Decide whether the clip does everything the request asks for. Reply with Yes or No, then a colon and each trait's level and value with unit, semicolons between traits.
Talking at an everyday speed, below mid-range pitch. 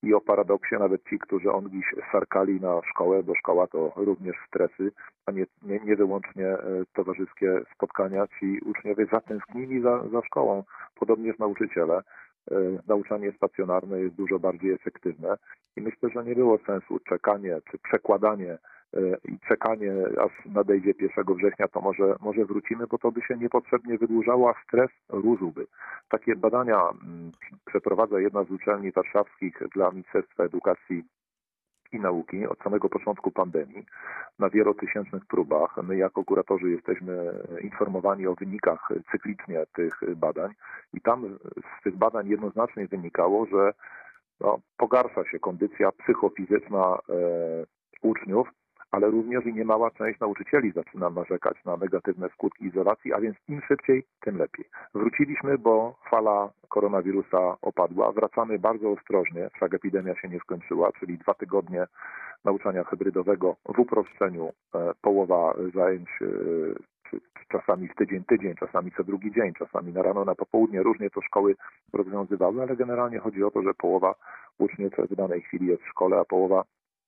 Yes: average, 145 wpm; low, 100 Hz